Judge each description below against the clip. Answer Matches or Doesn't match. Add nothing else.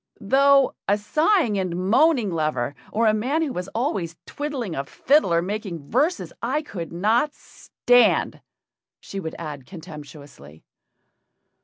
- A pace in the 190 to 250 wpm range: Doesn't match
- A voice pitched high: Matches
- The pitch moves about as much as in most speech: Doesn't match